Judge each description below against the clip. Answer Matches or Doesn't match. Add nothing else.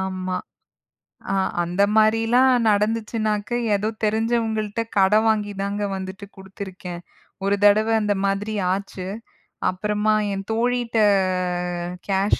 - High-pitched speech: Matches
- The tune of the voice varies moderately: Doesn't match